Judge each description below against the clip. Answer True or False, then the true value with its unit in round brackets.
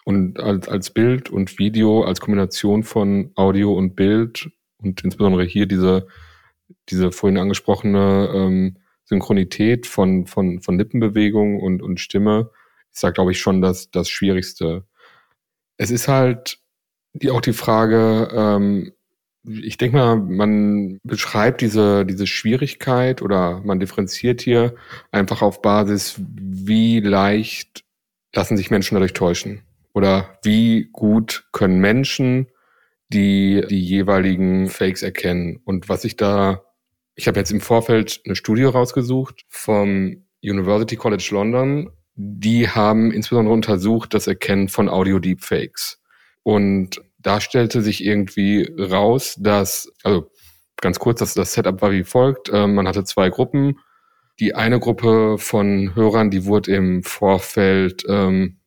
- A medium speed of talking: True (135 wpm)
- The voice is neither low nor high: False (100 Hz)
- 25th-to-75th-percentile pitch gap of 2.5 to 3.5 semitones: True (2.8 semitones)